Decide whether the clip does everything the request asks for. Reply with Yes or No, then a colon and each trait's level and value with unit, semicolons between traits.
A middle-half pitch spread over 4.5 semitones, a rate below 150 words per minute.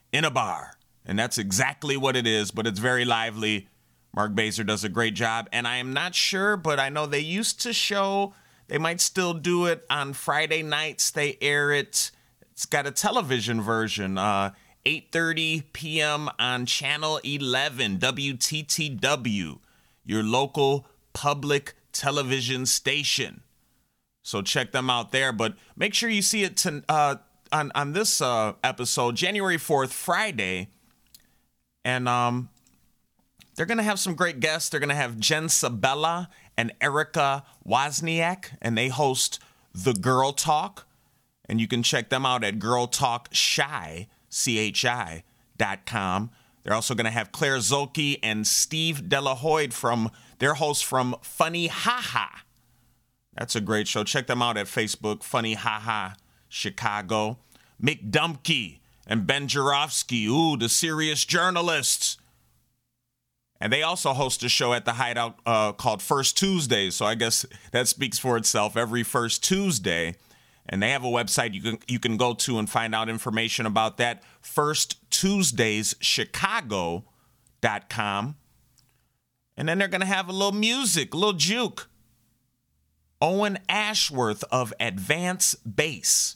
Yes: average, 5.1 semitones; average, 140 wpm